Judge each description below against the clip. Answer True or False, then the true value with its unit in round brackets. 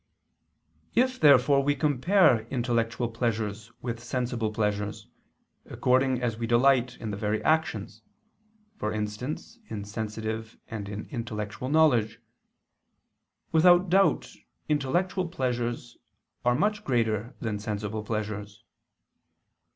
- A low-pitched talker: True (120 Hz)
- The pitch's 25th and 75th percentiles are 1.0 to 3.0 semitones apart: False (4.3 semitones)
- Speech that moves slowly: True (105 wpm)